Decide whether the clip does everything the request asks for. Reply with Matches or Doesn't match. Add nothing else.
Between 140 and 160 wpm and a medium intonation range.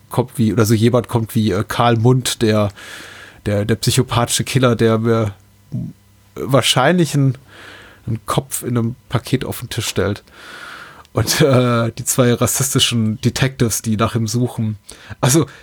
Doesn't match